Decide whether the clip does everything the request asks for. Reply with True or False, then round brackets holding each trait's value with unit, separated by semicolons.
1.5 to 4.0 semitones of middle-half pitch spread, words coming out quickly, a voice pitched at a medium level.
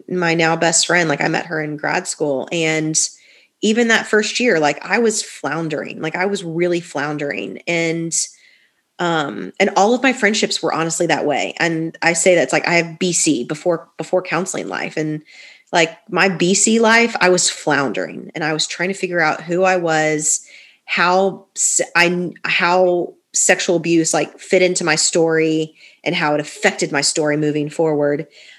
False (3.1 semitones; 180 wpm; 170 Hz)